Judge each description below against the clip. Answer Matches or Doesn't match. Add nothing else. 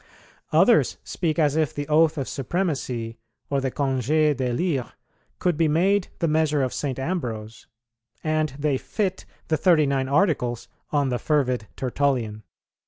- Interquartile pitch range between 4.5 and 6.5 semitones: Doesn't match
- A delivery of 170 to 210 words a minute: Doesn't match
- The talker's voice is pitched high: Doesn't match